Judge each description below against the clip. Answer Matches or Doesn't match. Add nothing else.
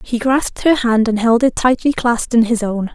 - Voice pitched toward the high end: Matches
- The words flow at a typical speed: Doesn't match